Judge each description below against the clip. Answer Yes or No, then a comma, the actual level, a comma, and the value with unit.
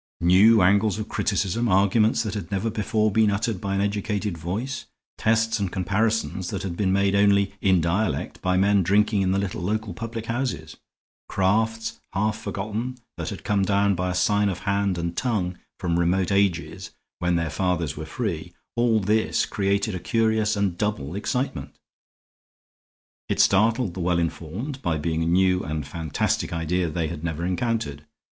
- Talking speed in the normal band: Yes, average, 165 wpm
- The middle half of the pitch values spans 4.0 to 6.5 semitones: No, average, 3.5 semitones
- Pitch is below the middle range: Yes, low, 100 Hz